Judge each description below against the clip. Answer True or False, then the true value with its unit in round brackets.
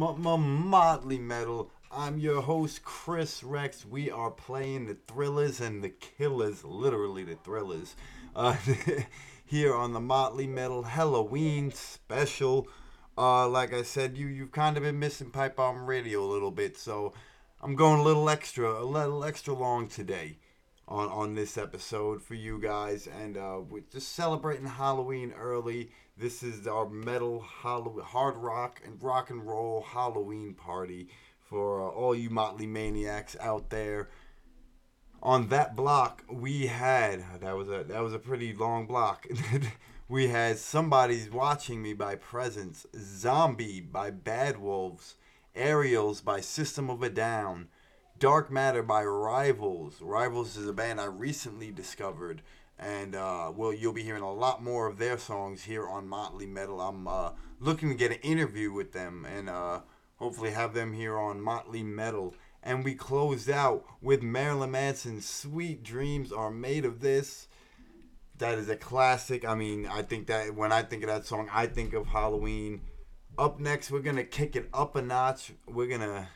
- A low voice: True (120 Hz)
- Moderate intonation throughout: True (4.1 semitones)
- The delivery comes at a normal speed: True (165 wpm)